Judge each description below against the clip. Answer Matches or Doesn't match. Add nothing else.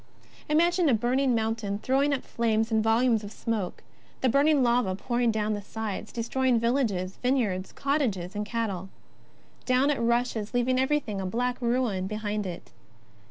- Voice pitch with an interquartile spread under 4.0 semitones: Matches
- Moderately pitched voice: Doesn't match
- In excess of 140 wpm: Matches